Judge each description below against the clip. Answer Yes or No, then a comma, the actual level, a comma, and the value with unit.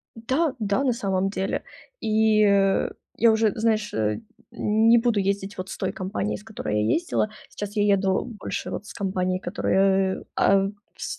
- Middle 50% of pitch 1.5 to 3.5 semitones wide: Yes, average, 2.7 semitones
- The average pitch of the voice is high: Yes, high, 205 Hz